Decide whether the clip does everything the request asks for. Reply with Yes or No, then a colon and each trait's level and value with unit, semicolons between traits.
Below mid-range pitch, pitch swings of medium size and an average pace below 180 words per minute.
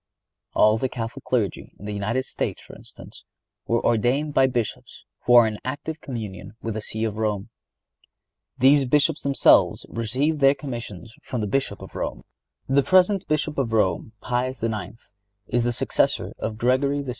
Yes: low, 120 Hz; average, 3.9 semitones; average, 170 wpm